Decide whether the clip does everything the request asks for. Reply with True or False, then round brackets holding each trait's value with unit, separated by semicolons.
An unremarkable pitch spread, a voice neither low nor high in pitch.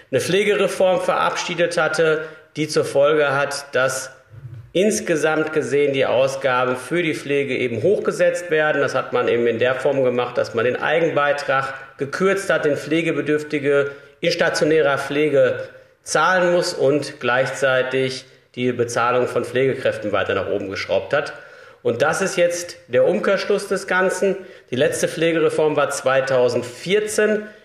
False (5.9 semitones; 155 Hz)